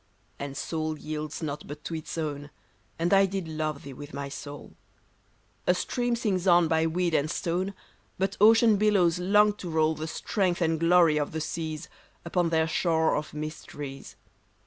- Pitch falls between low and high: Yes, medium, 160 Hz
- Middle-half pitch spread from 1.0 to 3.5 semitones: Yes, average, 2.9 semitones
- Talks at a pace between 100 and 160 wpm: No, average, 170 wpm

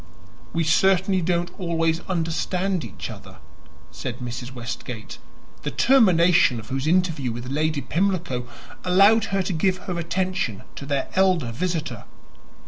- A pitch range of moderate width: No, wide, 6.0 semitones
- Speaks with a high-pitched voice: No, medium, 165 Hz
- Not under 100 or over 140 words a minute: Yes, slow, 135 wpm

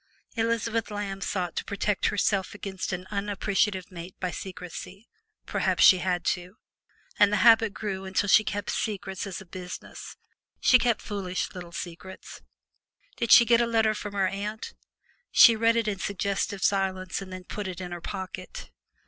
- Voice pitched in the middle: No, high, 195 Hz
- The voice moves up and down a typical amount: No, narrow, 2.3 semitones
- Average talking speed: Yes, average, 165 wpm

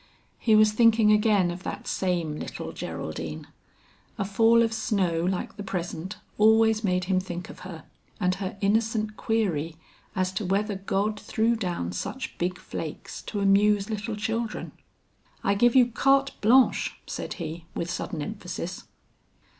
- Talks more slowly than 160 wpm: Yes, average, 150 wpm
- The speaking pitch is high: Yes, high, 200 Hz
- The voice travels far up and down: No, average, 3.5 semitones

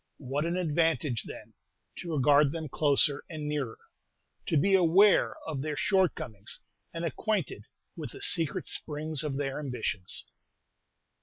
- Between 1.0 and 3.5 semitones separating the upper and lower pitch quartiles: Yes, average, 3.1 semitones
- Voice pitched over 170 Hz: No, medium, 150 Hz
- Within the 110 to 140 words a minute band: Yes, slow, 135 wpm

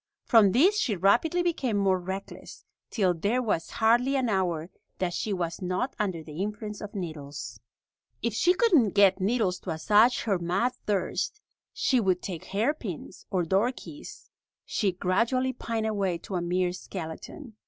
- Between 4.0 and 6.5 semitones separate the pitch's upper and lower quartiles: Yes, average, 4.7 semitones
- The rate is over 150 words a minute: Yes, average, 160 wpm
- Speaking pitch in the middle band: No, high, 200 Hz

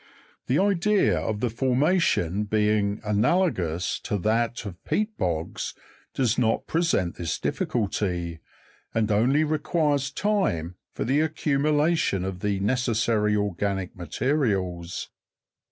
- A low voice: Yes, low, 110 Hz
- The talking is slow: Yes, slow, 110 wpm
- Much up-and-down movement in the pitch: Yes, wide, 7.3 semitones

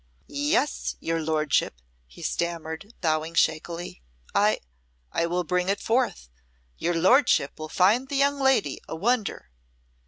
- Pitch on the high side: No, medium, 175 Hz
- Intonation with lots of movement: Yes, wide, 7.5 semitones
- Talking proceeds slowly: Yes, slow, 130 wpm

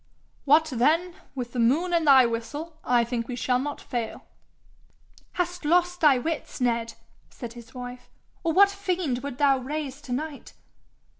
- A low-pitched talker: No, very high, 275 Hz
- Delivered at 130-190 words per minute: Yes, average, 160 wpm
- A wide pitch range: No, average, 4.8 semitones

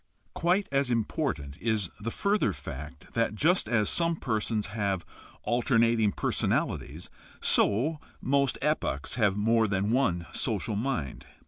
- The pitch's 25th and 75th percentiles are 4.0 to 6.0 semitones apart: Yes, average, 5.2 semitones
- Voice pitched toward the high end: No, low, 110 Hz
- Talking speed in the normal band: No, slow, 125 wpm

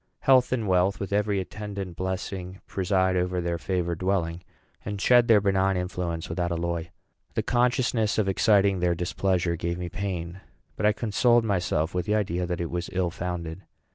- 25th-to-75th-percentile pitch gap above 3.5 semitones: No, average, 2.7 semitones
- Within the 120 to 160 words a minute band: No, average, 170 wpm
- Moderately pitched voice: No, very low, 95 Hz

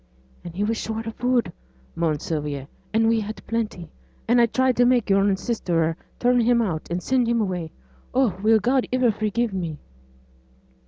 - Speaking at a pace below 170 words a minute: No, average, 175 wpm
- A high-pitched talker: Yes, high, 220 Hz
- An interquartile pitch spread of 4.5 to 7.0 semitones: Yes, average, 5.2 semitones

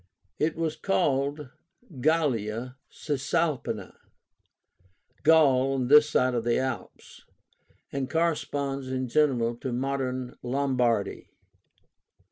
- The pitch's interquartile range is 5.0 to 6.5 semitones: No, average, 2.9 semitones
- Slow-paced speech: Yes, slow, 90 wpm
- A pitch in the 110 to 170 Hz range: Yes, low, 135 Hz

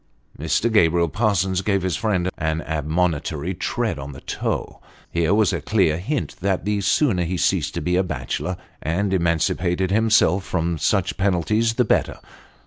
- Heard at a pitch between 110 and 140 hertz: No, very low, 90 Hz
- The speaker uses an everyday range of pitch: Yes, average, 3.5 semitones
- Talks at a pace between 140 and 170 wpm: Yes, average, 160 wpm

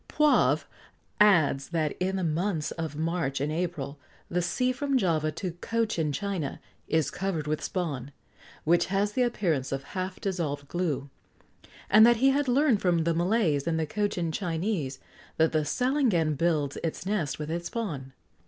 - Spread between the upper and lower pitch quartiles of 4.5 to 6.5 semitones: Yes, average, 4.9 semitones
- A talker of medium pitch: Yes, medium, 170 Hz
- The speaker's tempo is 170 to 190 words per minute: No, average, 160 wpm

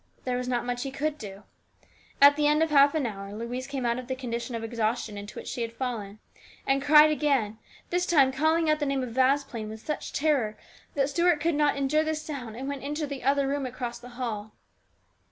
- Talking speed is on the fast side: Yes, fast, 225 wpm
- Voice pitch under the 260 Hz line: No, very high, 265 Hz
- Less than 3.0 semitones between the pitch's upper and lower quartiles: No, average, 3.8 semitones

